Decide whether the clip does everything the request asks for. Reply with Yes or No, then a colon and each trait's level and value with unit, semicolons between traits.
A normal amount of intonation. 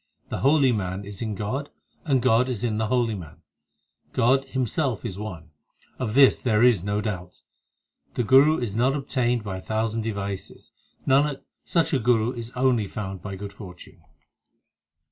Yes: average, 4.3 semitones